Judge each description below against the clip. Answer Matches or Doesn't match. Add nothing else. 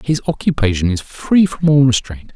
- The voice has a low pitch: Matches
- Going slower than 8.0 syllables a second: Matches